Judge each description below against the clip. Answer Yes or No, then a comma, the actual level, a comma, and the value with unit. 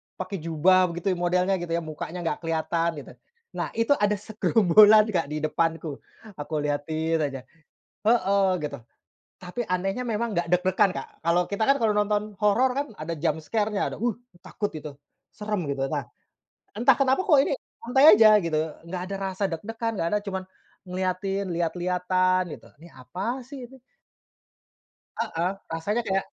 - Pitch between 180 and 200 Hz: Yes, medium, 185 Hz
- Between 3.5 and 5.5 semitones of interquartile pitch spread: Yes, average, 4.3 semitones